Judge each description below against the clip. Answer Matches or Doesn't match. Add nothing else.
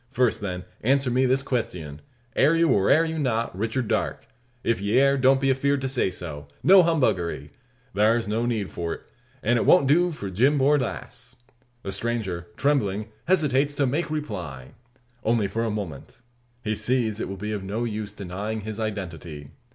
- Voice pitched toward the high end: Doesn't match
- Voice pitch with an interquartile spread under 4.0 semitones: Doesn't match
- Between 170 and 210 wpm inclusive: Matches